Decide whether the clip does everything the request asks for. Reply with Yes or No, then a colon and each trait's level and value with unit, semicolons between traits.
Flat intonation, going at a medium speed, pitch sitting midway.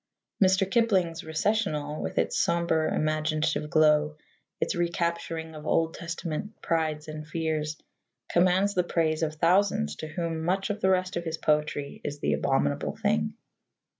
Yes: narrow, 2.2 semitones; average, 145 wpm; medium, 160 Hz